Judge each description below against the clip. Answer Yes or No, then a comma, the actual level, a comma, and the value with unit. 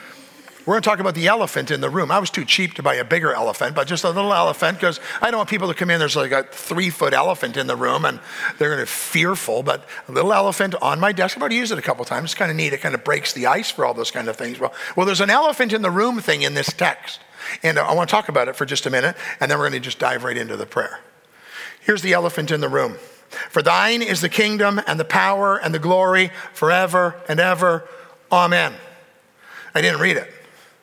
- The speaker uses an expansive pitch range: No, average, 3.5 semitones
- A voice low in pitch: No, medium, 185 Hz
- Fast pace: Yes, fast, 265 wpm